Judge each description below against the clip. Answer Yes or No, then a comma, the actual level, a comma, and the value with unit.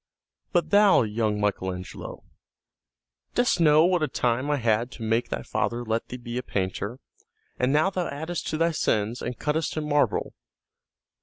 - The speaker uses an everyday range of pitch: No, wide, 5.8 semitones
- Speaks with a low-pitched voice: Yes, low, 125 Hz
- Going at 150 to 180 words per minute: Yes, average, 170 wpm